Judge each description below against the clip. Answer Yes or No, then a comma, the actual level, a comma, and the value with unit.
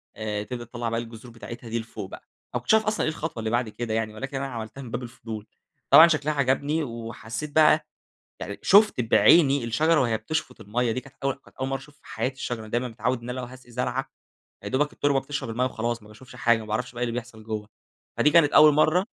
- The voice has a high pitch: No, low, 125 Hz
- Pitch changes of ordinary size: Yes, average, 3.8 semitones